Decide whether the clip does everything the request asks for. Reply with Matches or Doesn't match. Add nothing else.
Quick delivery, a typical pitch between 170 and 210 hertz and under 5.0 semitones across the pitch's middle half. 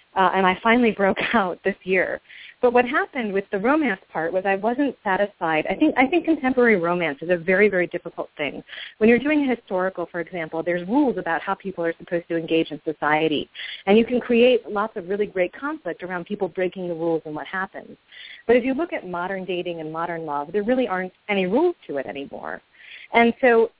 Doesn't match